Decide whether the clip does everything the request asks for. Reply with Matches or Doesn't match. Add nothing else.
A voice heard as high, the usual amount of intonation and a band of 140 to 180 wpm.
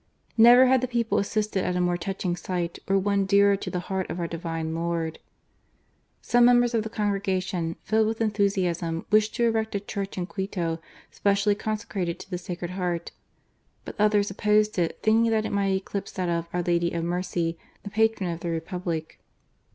Doesn't match